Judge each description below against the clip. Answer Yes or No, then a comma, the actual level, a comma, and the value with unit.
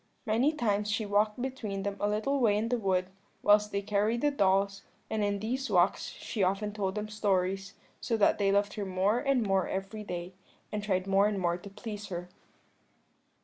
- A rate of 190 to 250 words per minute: Yes, average, 195 wpm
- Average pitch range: No, narrow, 1.9 semitones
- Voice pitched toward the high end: Yes, high, 205 Hz